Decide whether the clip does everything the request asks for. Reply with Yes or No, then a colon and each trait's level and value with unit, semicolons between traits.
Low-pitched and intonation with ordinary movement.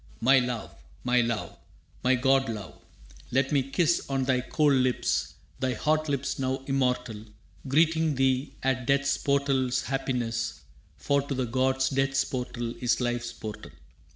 No: low, 130 Hz; narrow, 1.7 semitones